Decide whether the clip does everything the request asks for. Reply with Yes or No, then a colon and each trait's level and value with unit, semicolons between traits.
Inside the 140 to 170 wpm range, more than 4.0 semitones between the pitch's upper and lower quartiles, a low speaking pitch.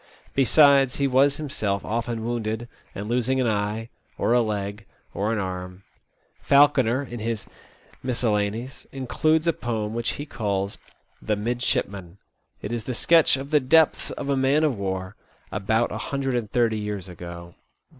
Yes: average, 165 wpm; average, 4.4 semitones; low, 115 Hz